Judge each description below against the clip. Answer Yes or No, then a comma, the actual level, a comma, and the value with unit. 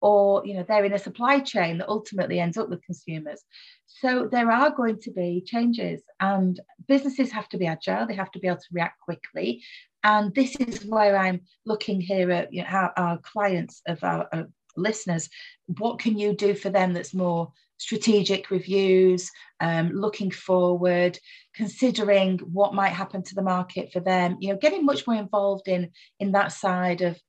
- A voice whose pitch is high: Yes, high, 195 Hz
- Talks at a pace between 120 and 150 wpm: No, average, 185 wpm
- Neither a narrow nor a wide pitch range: Yes, average, 3.0 semitones